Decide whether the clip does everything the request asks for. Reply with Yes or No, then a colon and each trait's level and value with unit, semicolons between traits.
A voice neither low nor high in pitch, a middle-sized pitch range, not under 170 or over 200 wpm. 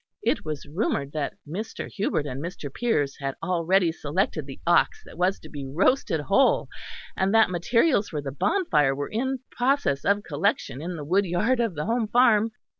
No: medium, 180 Hz; wide, 7.2 semitones; average, 180 wpm